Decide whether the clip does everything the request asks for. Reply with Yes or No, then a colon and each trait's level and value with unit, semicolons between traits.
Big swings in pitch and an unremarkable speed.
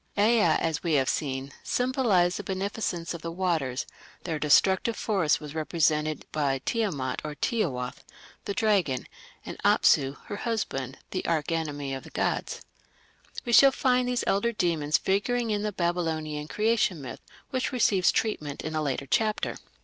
Yes: wide, 6.1 semitones; average, 155 wpm